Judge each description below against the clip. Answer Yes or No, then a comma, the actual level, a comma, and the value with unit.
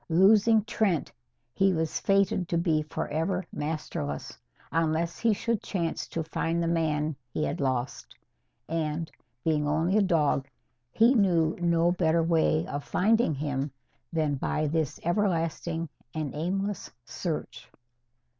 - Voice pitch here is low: No, medium, 165 Hz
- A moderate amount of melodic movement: Yes, average, 3.1 semitones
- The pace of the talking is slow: Yes, slow, 130 wpm